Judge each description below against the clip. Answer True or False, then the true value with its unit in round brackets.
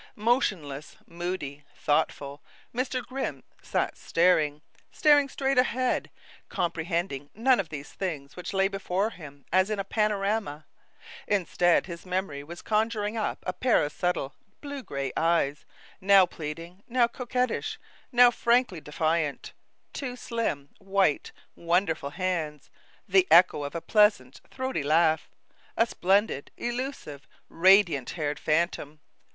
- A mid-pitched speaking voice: True (180 Hz)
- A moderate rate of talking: False (125 wpm)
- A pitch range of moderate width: False (6.2 semitones)